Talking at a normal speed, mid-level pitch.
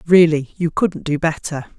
Yes: average, 170 wpm; medium, 160 Hz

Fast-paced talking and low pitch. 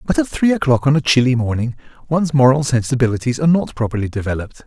No: average, 195 wpm; low, 130 Hz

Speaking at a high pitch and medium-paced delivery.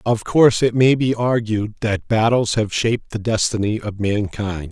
No: low, 110 Hz; average, 180 wpm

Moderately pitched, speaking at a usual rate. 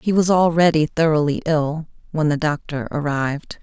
Yes: medium, 155 Hz; average, 150 wpm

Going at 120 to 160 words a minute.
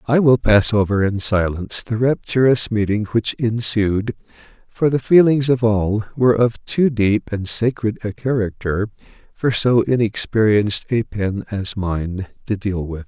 Yes: average, 155 wpm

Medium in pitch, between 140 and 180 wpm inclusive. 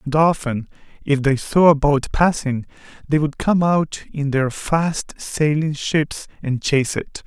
Yes: medium, 145 Hz; average, 165 wpm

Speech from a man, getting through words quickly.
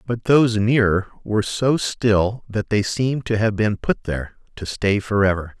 No: male; average, 180 wpm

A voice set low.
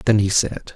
Yes: low, 105 Hz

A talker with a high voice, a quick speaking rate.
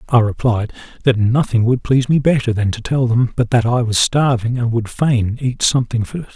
No: low, 120 Hz; fast, 215 wpm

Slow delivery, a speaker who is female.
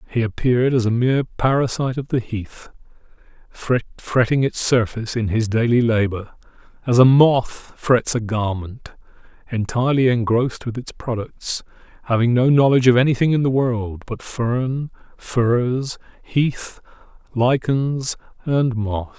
No: slow, 130 wpm; male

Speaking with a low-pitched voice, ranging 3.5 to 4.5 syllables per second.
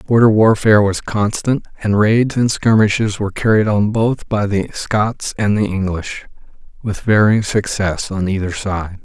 Yes: low, 105 Hz; 4.4 syllables/s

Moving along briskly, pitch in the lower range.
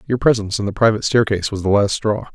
Yes: fast, 255 wpm; low, 105 Hz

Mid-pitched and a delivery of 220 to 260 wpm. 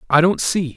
Yes: medium, 165 Hz; fast, 235 wpm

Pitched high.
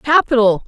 Yes: high, 235 Hz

